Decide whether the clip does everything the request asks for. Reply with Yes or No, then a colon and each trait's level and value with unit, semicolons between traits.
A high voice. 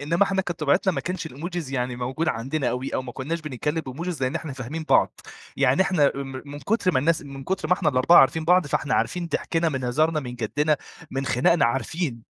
No: medium, 145 Hz